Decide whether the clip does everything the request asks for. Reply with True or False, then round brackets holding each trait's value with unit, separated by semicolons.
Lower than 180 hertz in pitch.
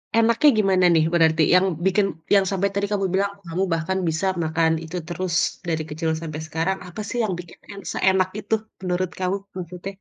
False (185 Hz)